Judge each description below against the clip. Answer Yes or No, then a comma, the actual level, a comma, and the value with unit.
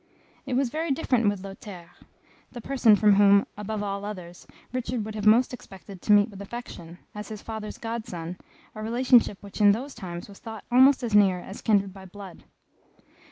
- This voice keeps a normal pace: Yes, average, 190 wpm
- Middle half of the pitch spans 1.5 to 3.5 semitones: Yes, average, 3.0 semitones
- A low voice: No, high, 210 Hz